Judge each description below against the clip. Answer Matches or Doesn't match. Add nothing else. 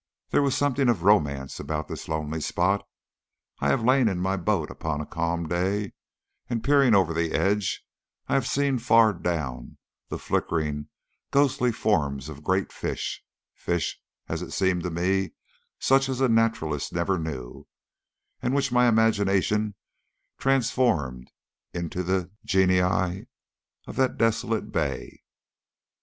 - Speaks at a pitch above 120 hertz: Doesn't match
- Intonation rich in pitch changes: Matches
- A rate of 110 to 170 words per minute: Matches